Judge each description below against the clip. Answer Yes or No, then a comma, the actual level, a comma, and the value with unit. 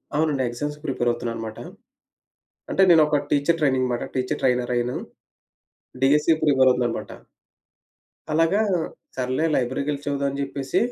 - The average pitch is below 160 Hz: Yes, low, 135 Hz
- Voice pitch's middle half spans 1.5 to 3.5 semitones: Yes, average, 3.0 semitones